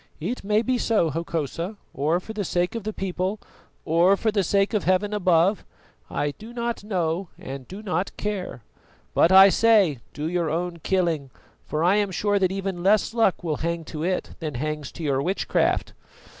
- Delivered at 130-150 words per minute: No, average, 185 wpm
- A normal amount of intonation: Yes, average, 4.0 semitones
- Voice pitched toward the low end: No, medium, 185 Hz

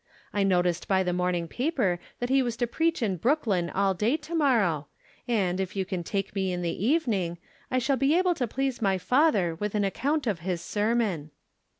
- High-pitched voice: Yes, high, 205 Hz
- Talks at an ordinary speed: No, fast, 210 wpm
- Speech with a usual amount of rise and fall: No, wide, 6.3 semitones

